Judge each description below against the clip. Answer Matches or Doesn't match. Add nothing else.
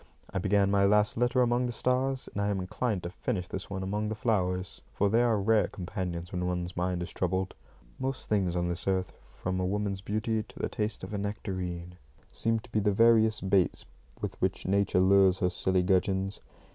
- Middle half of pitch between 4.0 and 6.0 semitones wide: Doesn't match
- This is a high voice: Doesn't match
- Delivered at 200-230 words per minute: Matches